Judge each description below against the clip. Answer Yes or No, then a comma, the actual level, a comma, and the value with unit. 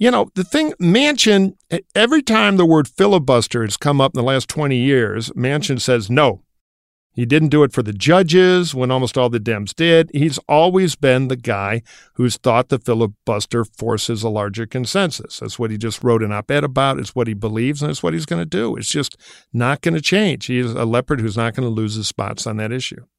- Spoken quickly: Yes, fast, 220 wpm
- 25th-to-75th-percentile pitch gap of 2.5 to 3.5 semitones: No, average, 4.8 semitones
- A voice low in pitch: Yes, low, 125 Hz